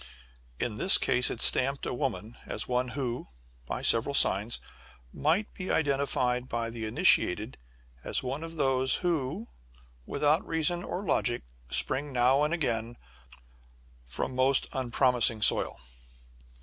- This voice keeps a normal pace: No, slow, 130 wpm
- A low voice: Yes, low, 130 Hz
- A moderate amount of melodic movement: Yes, average, 3.8 semitones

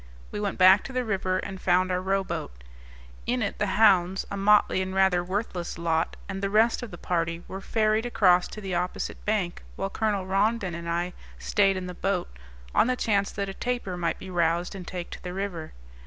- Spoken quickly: Yes, fast, 210 wpm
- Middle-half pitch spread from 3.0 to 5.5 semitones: No, narrow, 2.5 semitones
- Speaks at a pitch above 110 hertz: Yes, high, 190 Hz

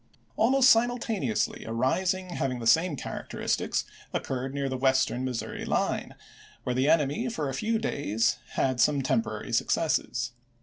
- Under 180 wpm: Yes, average, 140 wpm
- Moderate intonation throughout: No, wide, 6.6 semitones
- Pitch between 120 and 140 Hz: Yes, low, 135 Hz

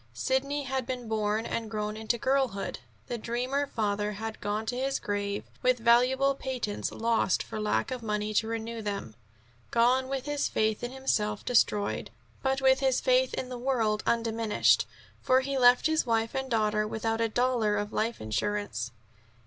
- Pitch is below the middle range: No, high, 230 Hz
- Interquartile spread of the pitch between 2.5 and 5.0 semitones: Yes, average, 3.4 semitones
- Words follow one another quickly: No, average, 170 wpm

